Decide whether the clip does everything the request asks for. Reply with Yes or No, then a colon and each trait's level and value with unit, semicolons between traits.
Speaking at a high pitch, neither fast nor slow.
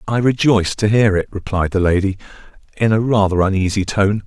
No: low, 100 Hz; average, 185 wpm